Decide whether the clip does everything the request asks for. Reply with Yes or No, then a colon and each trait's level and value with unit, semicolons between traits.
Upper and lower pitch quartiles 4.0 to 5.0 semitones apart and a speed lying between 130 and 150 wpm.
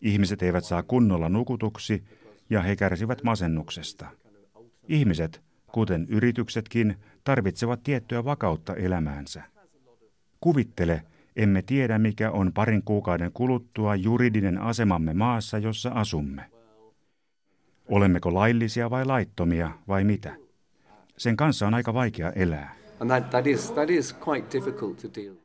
No: average, 4.5 semitones; slow, 95 wpm